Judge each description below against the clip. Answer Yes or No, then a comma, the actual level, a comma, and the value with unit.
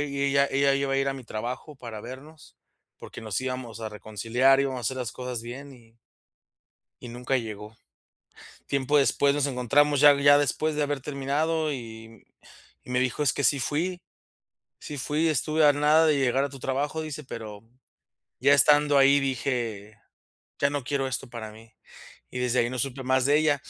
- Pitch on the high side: No, low, 135 Hz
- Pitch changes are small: No, average, 3.1 semitones